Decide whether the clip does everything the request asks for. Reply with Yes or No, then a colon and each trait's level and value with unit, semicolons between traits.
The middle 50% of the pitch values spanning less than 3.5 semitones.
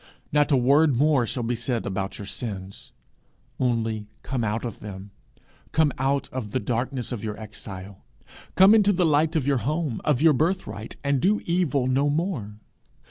No: wide, 5.4 semitones